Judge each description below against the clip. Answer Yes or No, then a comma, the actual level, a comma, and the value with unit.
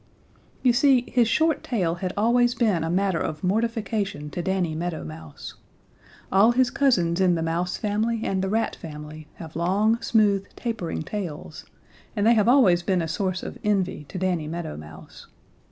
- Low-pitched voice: No, high, 190 Hz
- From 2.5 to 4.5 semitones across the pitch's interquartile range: No, average, 5.1 semitones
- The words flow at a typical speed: Yes, average, 170 wpm